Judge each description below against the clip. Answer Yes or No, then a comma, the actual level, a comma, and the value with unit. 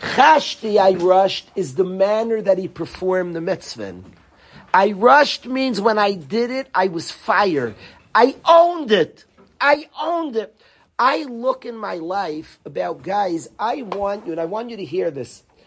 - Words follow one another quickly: No, average, 170 wpm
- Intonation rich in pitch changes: Yes, wide, 5.9 semitones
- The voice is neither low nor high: No, high, 205 Hz